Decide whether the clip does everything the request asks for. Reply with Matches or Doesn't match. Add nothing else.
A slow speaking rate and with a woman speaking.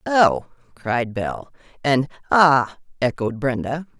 Matches